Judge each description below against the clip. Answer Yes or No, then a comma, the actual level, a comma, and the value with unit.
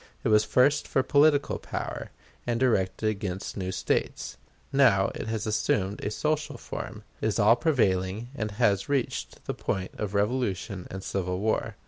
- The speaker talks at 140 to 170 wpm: Yes, average, 155 wpm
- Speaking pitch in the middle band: No, low, 110 Hz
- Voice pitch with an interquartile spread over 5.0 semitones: No, average, 4.5 semitones